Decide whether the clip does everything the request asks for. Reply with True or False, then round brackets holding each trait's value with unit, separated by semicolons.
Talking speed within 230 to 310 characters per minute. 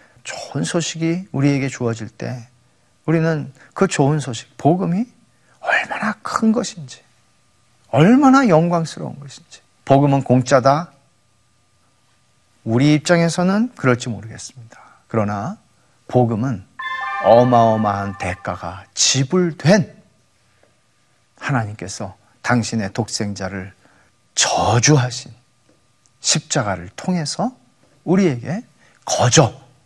False (220 characters per minute)